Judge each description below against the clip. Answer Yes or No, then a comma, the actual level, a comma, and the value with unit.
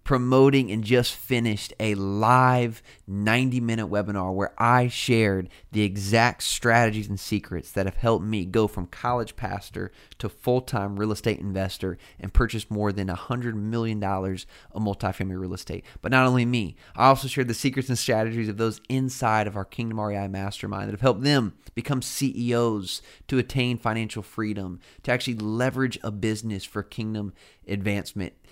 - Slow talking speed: No, average, 165 wpm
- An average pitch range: Yes, average, 3.5 semitones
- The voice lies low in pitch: Yes, low, 110 Hz